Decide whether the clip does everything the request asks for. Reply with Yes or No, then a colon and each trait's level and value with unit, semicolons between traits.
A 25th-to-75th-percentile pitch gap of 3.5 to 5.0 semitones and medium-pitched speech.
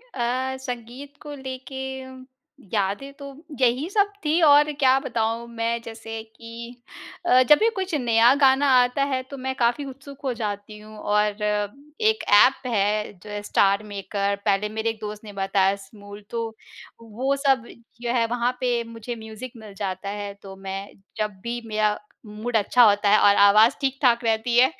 No: average, 3.9 semitones; high, 230 Hz